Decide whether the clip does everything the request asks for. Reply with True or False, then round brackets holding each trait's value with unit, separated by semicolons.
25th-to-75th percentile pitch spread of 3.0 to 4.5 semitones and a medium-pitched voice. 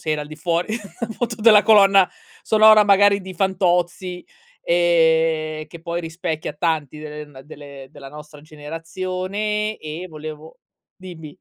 True (3.7 semitones; 170 Hz)